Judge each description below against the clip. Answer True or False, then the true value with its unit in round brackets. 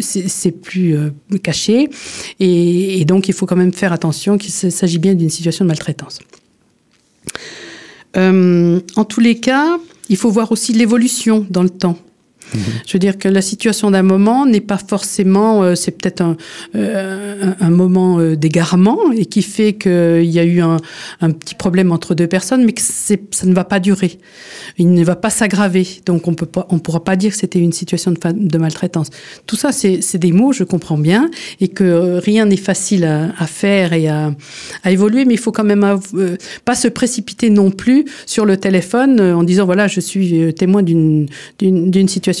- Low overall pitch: False (190 Hz)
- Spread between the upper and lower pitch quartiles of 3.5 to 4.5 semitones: False (3.0 semitones)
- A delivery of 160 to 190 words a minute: False (200 wpm)